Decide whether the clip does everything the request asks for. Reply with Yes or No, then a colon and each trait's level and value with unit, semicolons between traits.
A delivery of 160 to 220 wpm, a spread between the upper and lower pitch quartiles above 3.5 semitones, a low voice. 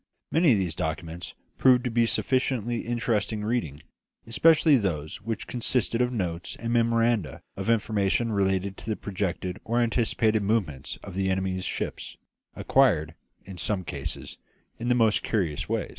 No: average, 150 wpm; average, 4.1 semitones; low, 110 Hz